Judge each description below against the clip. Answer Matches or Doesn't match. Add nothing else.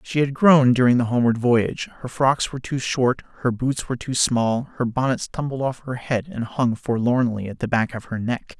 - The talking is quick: Matches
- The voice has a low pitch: Matches